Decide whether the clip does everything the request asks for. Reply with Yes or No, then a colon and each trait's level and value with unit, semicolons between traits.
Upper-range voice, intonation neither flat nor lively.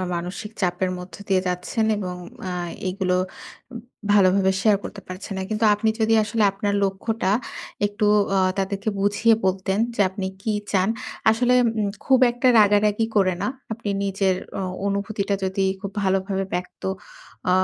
No: high, 200 Hz; narrow, 2.0 semitones